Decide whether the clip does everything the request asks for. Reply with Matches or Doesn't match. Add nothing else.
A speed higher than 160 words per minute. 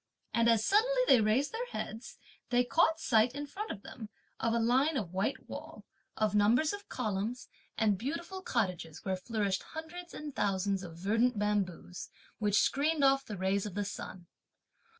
Matches